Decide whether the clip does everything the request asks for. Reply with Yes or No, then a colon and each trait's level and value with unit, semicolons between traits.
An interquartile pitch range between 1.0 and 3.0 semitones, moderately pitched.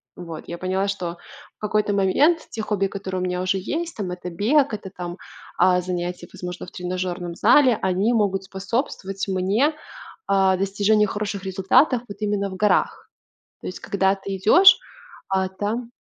No: narrow, 2.4 semitones; high, 195 Hz